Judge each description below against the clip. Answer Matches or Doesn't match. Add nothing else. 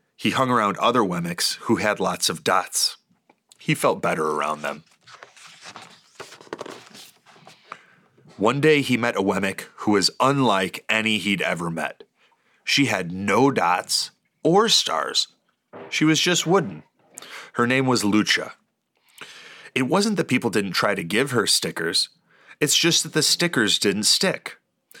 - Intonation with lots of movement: Matches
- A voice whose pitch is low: Matches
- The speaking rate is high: Doesn't match